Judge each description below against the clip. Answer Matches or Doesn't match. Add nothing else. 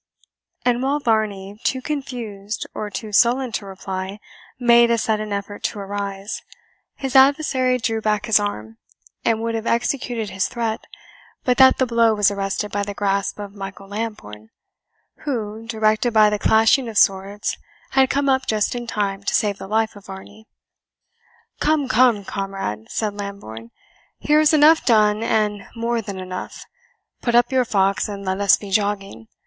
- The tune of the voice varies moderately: Matches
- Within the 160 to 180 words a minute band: Matches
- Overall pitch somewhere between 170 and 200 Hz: Doesn't match